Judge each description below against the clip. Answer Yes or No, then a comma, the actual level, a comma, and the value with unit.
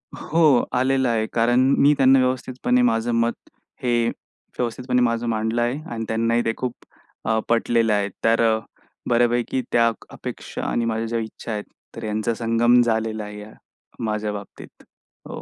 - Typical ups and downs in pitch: No, narrow, 1.6 semitones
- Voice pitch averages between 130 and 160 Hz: No, low, 115 Hz